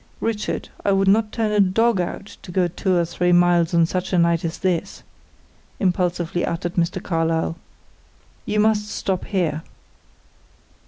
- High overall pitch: No, medium, 180 Hz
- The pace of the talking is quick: No, average, 155 wpm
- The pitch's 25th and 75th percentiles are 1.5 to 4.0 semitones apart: Yes, average, 2.7 semitones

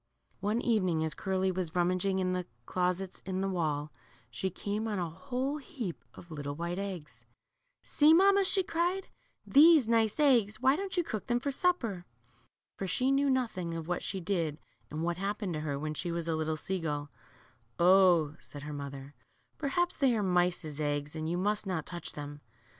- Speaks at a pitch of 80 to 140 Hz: No, medium, 185 Hz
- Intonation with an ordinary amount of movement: No, wide, 6.5 semitones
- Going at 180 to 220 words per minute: Yes, average, 185 wpm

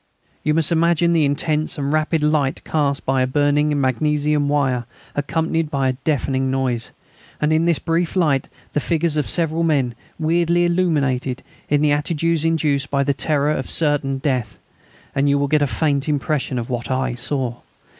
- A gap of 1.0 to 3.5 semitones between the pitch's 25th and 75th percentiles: Yes, average, 2.7 semitones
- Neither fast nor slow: Yes, average, 175 wpm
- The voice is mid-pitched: Yes, medium, 145 Hz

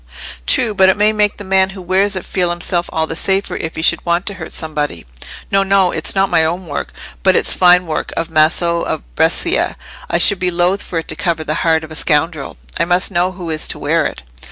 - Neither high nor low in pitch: Yes, medium, 175 Hz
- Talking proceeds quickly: Yes, fast, 240 wpm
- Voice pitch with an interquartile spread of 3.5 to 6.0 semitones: No, average, 3.0 semitones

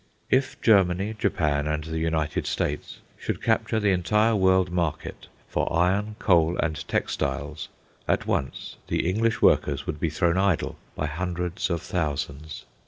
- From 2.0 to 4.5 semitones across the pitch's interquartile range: Yes, average, 3.8 semitones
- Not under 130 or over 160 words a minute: Yes, average, 145 wpm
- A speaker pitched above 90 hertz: No, very low, 85 Hz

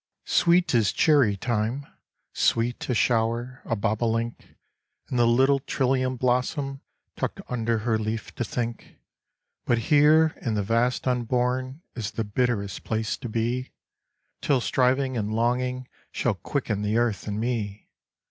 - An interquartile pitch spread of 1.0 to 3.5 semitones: Yes, narrow, 2.4 semitones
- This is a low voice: Yes, low, 120 Hz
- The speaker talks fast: No, average, 140 wpm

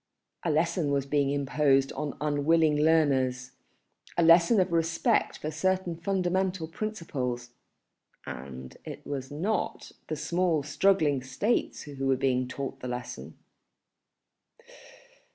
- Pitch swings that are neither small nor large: Yes, average, 4.0 semitones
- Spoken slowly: Yes, slow, 115 wpm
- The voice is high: No, medium, 150 Hz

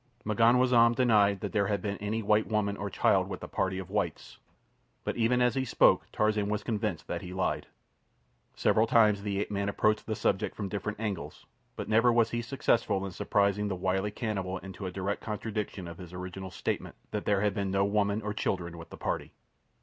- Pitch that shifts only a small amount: Yes, narrow, 2.1 semitones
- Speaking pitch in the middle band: No, low, 105 Hz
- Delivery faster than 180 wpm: Yes, fast, 205 wpm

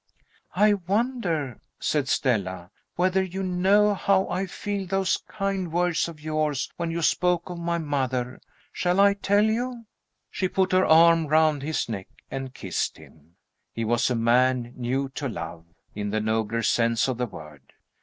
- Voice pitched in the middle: Yes, medium, 160 Hz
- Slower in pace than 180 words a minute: Yes, average, 165 wpm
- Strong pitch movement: Yes, wide, 7.6 semitones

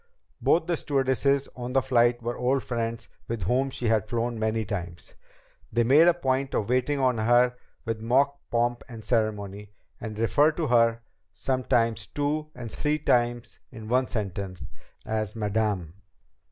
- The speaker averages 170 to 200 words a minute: No, average, 155 wpm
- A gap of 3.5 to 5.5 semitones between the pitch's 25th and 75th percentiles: No, average, 3.1 semitones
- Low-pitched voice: Yes, low, 120 Hz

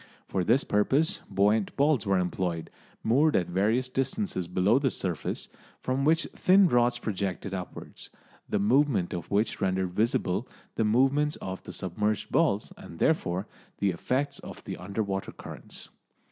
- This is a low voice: Yes, low, 105 Hz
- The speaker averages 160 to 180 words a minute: No, average, 150 wpm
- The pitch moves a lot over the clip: Yes, wide, 6.0 semitones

